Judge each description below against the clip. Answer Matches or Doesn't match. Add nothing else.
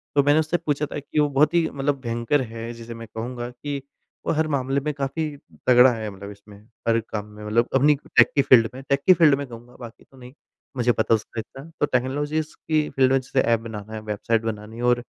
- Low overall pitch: Matches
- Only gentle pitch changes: Doesn't match